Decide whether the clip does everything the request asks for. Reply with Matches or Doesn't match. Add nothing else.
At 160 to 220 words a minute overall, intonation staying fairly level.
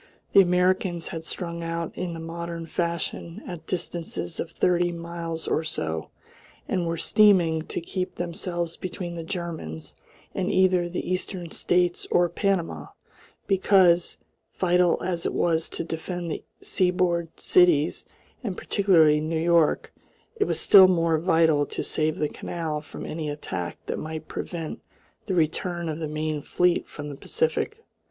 Doesn't match